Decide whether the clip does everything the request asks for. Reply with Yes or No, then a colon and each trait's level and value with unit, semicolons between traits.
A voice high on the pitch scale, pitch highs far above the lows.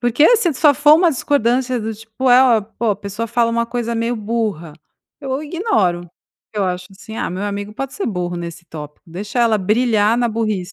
No: high, 225 Hz; average, 3.8 semitones